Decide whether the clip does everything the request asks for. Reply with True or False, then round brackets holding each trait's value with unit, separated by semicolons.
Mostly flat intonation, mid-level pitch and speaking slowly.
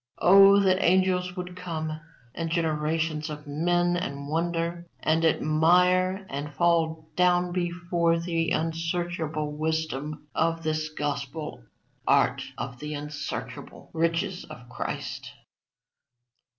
True (2.3 semitones; 165 Hz; 110 wpm)